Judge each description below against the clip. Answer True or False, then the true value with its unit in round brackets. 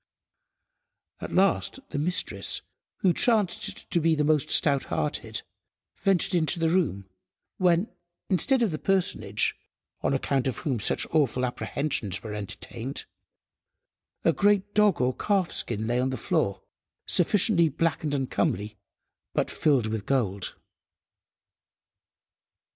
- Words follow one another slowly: True (120 wpm)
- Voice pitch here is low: False (150 Hz)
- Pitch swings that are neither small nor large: False (6.8 semitones)